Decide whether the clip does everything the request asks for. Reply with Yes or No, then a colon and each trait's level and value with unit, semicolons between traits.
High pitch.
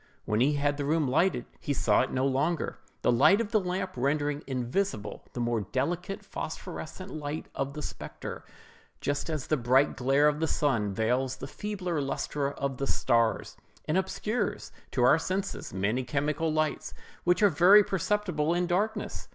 No: medium, 145 Hz